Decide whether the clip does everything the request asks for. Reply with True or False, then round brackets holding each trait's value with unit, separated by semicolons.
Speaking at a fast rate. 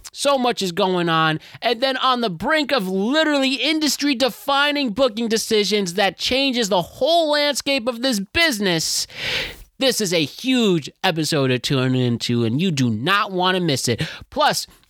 False (165 wpm)